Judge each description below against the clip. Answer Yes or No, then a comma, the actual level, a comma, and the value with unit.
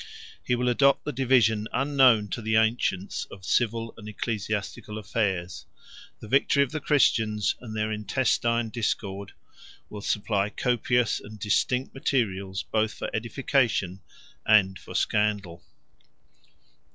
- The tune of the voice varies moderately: Yes, average, 3.0 semitones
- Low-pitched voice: Yes, low, 110 Hz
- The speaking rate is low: Yes, slow, 125 wpm